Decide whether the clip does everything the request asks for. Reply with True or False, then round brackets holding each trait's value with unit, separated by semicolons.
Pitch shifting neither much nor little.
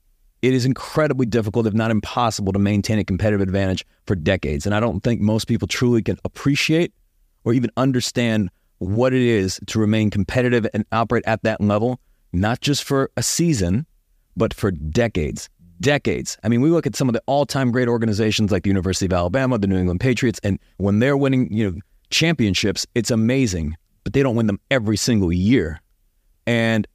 True (4.2 semitones)